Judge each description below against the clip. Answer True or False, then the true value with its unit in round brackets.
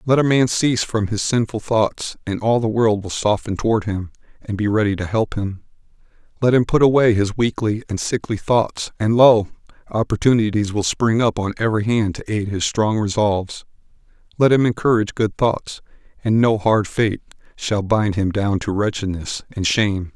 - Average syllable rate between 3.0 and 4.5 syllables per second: False (5.0 syllables/s)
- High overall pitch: False (110 Hz)